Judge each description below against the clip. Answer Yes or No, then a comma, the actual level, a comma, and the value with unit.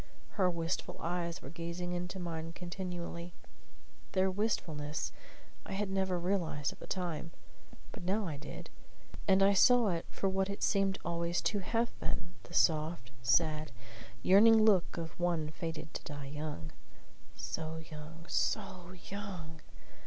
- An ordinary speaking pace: Yes, average, 145 wpm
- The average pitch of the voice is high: No, medium, 175 Hz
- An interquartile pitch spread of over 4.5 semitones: No, average, 3.1 semitones